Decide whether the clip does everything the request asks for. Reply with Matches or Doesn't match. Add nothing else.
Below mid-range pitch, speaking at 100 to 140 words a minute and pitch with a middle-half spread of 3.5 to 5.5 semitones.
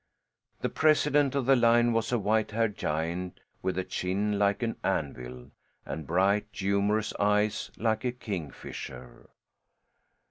Matches